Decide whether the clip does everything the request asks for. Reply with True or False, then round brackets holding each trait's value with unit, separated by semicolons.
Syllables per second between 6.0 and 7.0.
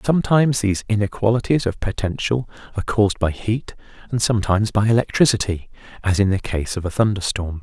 True (6.3 syllables/s)